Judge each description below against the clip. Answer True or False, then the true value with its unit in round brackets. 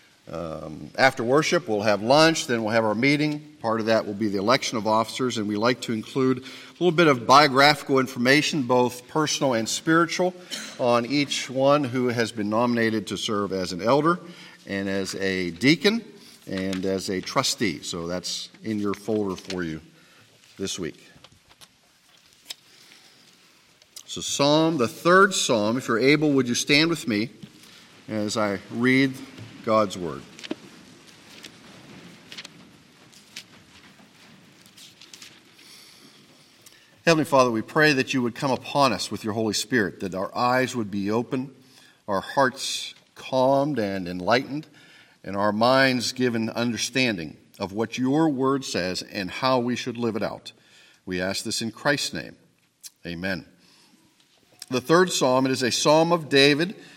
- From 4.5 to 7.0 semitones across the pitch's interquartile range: True (5.0 semitones)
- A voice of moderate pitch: False (125 Hz)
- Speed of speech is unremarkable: True (145 wpm)